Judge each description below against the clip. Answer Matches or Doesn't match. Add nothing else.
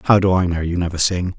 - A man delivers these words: Matches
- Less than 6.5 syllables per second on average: Doesn't match